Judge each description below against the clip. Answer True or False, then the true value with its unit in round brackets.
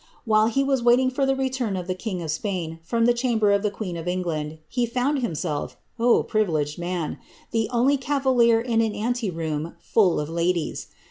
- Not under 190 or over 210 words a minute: True (200 wpm)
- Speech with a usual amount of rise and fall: False (6.0 semitones)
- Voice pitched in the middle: False (215 Hz)